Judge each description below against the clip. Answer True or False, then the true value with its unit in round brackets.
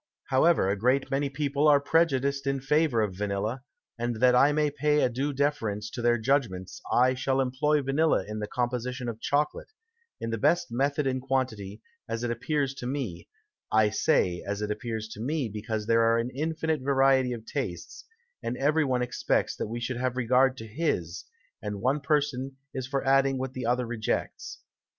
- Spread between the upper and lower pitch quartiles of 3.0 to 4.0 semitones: True (3.5 semitones)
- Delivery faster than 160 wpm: True (185 wpm)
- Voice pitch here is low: True (130 Hz)